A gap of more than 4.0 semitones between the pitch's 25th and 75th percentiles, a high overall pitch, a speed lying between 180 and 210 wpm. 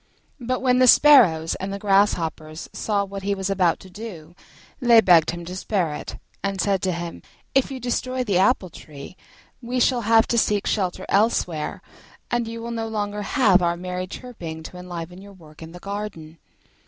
Yes: average, 4.6 semitones; high, 195 Hz; average, 185 wpm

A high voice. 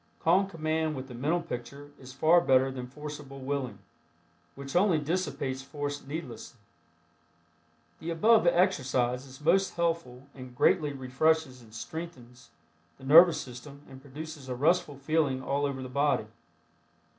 No: medium, 140 Hz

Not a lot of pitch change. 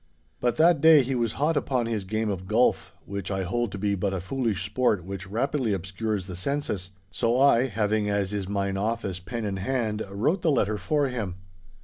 No: average, 4.3 semitones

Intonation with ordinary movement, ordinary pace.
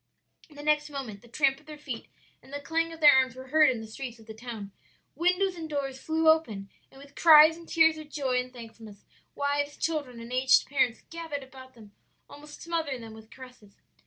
No: average, 4.2 semitones; fast, 210 wpm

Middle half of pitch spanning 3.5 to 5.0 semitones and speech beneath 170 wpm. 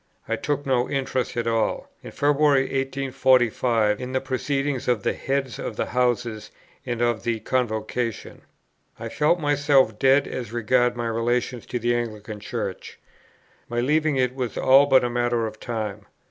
No: narrow, 2.6 semitones; average, 160 wpm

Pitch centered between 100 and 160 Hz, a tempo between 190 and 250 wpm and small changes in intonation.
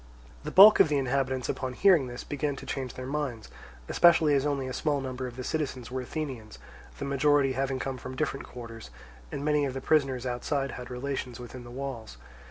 Yes: low, 135 Hz; average, 200 wpm; narrow, 2.3 semitones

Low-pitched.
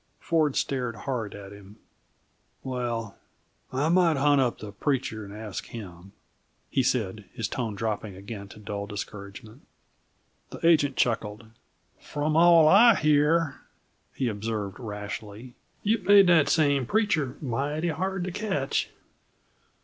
Yes: low, 125 Hz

